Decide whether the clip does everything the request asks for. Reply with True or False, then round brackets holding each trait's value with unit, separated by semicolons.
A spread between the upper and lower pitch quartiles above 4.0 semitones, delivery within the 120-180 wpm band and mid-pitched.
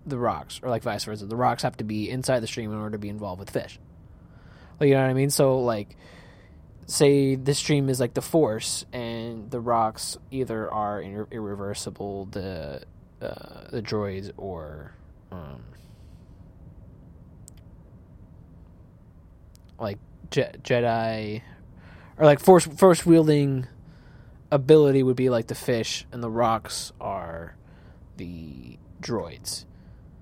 False (5.6 semitones; 135 wpm; 110 Hz)